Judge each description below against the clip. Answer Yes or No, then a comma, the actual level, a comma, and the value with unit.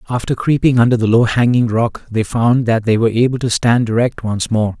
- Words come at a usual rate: No, fast, 225 wpm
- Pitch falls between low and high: No, low, 115 Hz